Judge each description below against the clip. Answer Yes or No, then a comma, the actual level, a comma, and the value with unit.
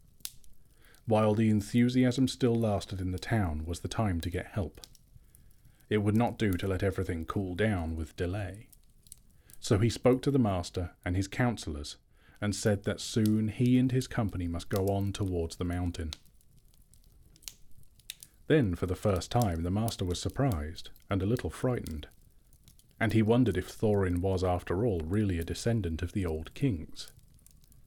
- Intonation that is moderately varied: Yes, average, 4.5 semitones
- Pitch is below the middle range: Yes, low, 100 Hz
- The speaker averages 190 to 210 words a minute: No, average, 165 wpm